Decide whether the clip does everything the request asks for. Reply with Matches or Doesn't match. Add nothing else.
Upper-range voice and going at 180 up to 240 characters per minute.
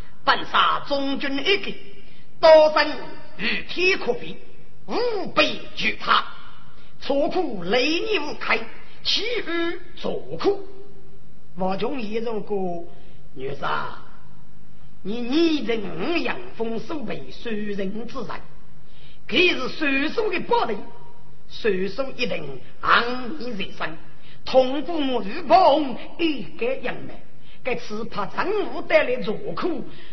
Doesn't match